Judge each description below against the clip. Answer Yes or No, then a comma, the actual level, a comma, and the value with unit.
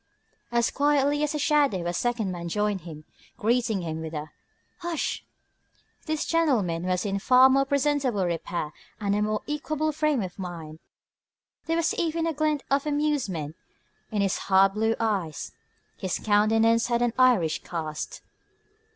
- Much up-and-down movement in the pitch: Yes, wide, 7.9 semitones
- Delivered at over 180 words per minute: No, average, 150 wpm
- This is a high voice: Yes, high, 225 Hz